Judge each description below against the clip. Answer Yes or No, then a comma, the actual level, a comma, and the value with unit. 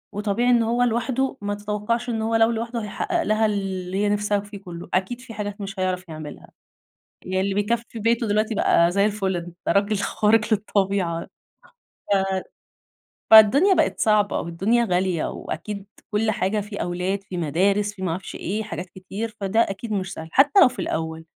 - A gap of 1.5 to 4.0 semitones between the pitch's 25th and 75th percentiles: Yes, average, 3.1 semitones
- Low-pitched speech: No, high, 205 Hz